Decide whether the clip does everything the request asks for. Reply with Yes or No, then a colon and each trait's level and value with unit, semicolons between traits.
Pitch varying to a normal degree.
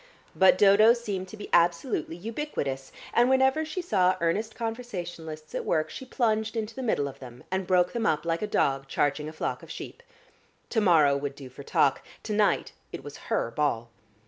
No: wide, 6.8 semitones